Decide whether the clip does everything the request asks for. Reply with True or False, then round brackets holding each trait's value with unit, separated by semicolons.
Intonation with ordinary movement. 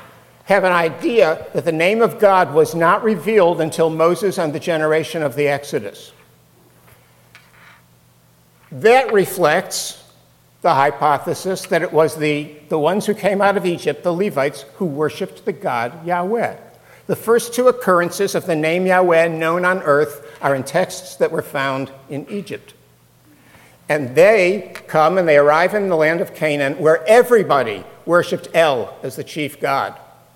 True (4.7 semitones)